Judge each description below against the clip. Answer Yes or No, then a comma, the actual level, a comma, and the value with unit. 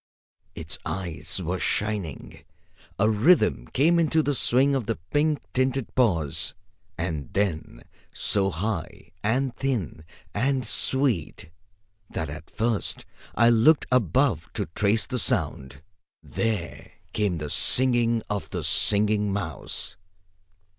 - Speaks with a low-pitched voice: Yes, low, 105 Hz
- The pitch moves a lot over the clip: Yes, wide, 7.2 semitones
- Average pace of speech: No, slow, 120 wpm